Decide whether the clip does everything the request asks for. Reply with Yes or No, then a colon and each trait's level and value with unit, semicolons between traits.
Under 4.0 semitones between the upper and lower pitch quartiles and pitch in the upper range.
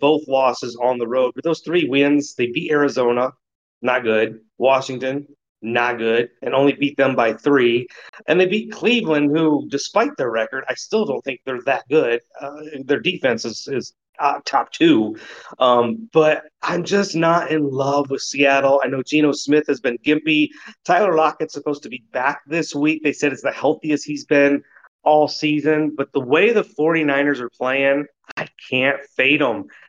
No: average, 2.8 semitones; medium, 140 Hz